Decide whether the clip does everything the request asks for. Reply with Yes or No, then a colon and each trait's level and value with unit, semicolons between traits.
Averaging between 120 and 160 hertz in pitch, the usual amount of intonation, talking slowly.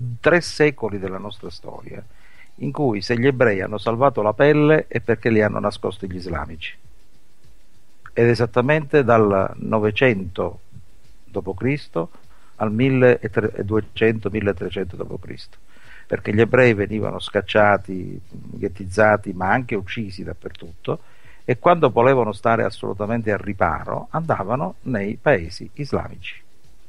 No: low, 105 Hz; average, 3.5 semitones; slow, 110 wpm